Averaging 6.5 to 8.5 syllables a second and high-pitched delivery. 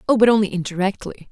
Yes: 7.0 syllables/s; high, 200 Hz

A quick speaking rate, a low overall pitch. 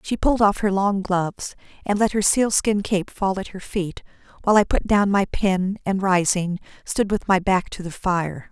No: fast, 210 wpm; high, 195 Hz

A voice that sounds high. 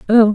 Yes: high, 220 Hz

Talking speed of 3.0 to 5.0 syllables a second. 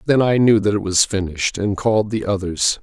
No: 5.6 syllables/s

